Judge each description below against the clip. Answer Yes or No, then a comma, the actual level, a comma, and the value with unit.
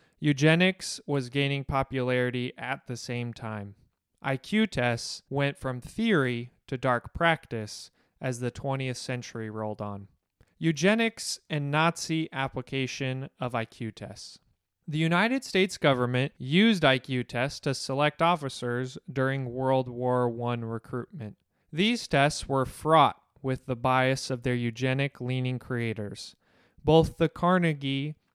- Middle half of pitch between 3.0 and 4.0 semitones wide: Yes, average, 3.7 semitones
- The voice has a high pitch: No, low, 130 Hz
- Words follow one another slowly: Yes, slow, 125 wpm